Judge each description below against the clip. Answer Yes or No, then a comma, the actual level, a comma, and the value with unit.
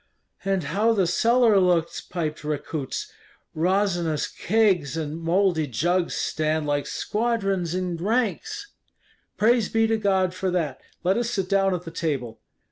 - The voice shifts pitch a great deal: No, average, 4.2 semitones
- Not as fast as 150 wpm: Yes, average, 140 wpm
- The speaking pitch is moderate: Yes, medium, 180 Hz